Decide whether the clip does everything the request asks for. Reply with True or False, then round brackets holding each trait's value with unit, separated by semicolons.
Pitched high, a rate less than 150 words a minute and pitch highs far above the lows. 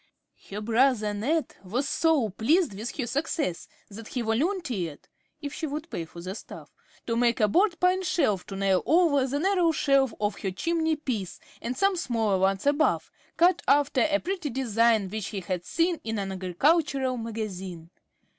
False (245 Hz; 175 wpm; 7.7 semitones)